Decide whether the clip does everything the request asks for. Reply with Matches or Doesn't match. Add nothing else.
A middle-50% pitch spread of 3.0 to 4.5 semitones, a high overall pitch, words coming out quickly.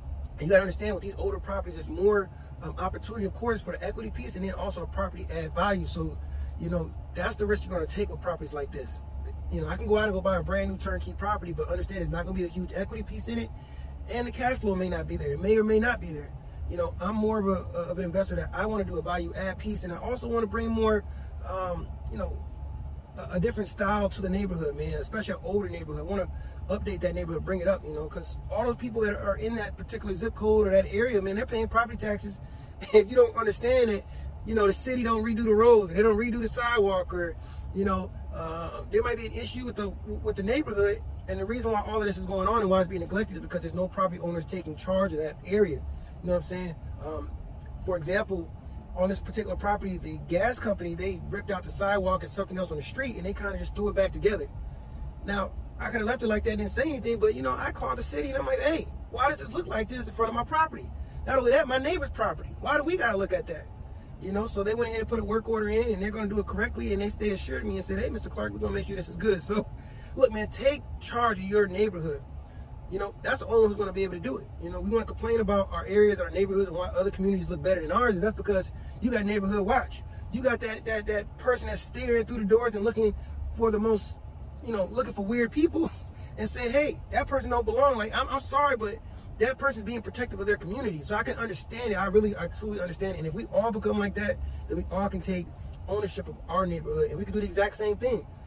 Matches